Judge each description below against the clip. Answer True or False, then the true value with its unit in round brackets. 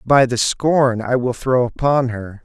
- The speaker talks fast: False (195 wpm)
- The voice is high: False (125 Hz)